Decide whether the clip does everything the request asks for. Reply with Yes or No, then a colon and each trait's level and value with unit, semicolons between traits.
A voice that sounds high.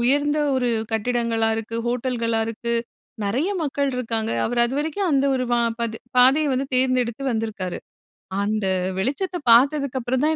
Yes: very high, 250 Hz